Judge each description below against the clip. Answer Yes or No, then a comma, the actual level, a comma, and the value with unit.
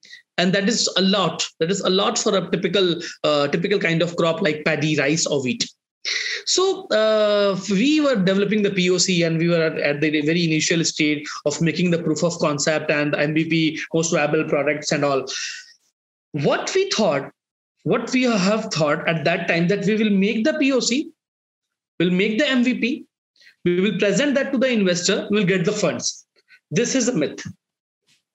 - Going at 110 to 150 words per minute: No, average, 185 wpm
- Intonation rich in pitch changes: Yes, wide, 6.0 semitones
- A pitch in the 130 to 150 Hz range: No, high, 190 Hz